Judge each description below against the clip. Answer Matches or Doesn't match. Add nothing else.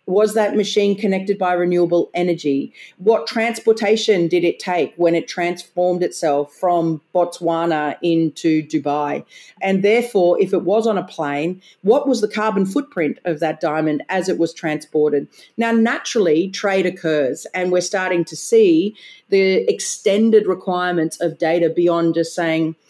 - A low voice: Doesn't match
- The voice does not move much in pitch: Doesn't match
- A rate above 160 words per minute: Doesn't match